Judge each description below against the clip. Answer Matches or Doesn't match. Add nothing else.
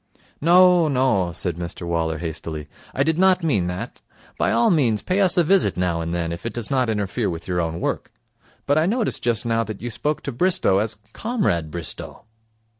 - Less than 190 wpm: Doesn't match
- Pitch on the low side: Matches